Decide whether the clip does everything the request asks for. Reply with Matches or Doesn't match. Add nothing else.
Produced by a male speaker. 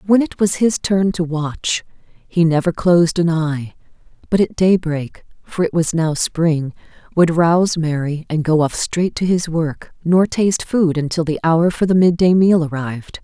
Doesn't match